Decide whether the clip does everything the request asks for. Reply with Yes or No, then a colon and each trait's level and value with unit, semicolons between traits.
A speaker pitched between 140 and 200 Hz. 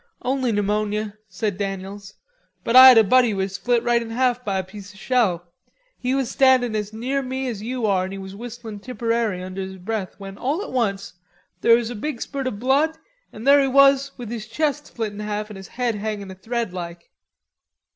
No: high, 225 Hz